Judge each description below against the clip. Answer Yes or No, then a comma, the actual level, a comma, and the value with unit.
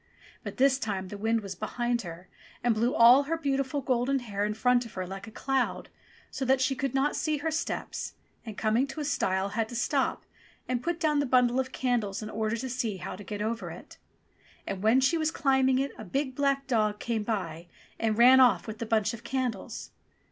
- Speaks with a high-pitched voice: Yes, high, 240 Hz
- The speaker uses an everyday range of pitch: Yes, average, 3.8 semitones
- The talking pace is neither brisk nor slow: No, fast, 220 wpm